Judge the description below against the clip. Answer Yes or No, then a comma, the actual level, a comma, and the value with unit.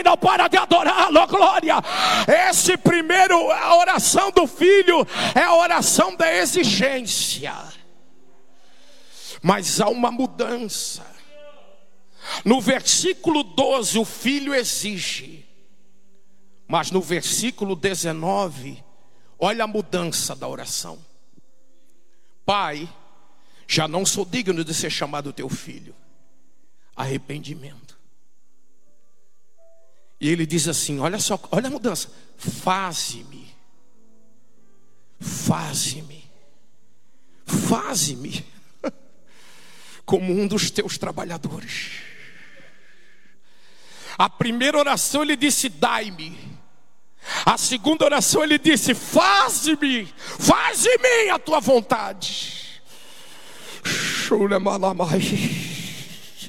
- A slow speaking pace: Yes, slow, 85 wpm